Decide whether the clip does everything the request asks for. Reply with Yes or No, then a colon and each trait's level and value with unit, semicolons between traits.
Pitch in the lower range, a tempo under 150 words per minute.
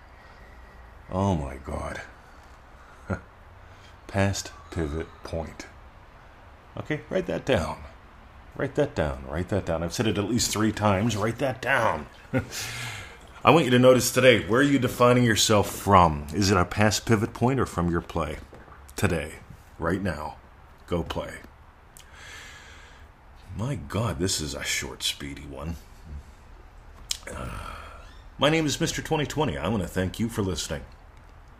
Yes: very low, 95 Hz; average, 140 wpm